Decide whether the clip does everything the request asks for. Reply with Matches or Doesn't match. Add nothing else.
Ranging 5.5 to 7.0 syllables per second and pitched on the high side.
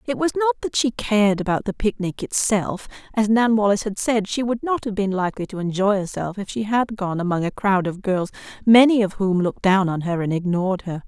Matches